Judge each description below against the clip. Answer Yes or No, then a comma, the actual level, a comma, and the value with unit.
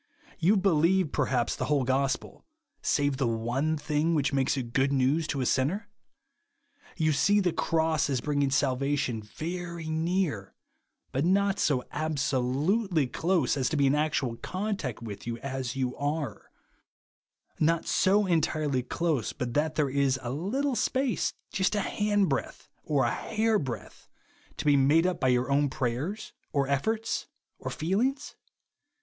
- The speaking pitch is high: No, medium, 150 Hz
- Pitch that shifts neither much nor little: Yes, average, 5.0 semitones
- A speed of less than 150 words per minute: No, average, 155 wpm